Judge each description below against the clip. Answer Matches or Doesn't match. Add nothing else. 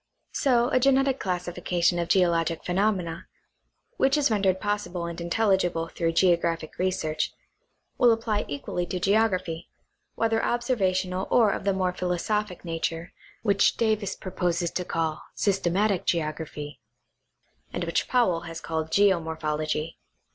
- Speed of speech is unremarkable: Doesn't match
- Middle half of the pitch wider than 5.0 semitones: Doesn't match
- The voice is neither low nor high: Matches